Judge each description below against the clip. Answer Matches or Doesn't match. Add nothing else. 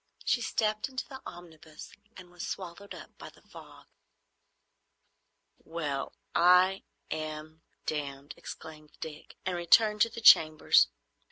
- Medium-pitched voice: Matches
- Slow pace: Matches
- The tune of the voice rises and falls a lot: Doesn't match